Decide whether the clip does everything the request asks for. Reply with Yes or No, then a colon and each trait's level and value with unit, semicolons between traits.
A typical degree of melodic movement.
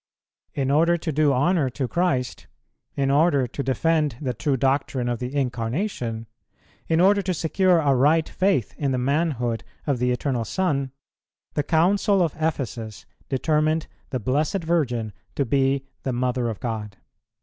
Yes: average, 4.4 semitones